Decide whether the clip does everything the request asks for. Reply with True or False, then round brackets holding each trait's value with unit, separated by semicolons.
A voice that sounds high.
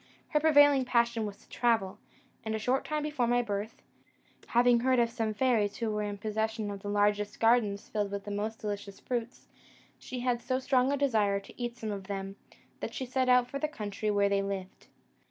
True (220 Hz)